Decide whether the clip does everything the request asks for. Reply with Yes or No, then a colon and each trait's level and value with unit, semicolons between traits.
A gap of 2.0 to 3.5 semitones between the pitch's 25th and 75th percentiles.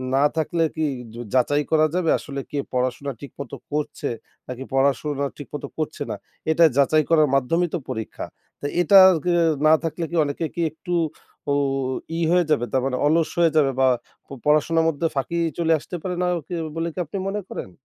Yes: average, 3.1 semitones